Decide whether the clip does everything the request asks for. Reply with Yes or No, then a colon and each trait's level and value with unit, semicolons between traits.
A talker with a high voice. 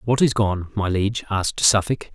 No: low, 105 Hz